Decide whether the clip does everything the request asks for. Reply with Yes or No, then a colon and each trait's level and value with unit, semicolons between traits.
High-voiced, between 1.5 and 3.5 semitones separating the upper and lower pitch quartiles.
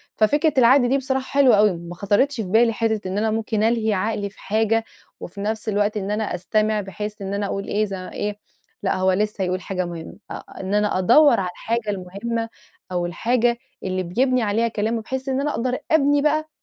Yes: high, 215 Hz; average, 3.1 semitones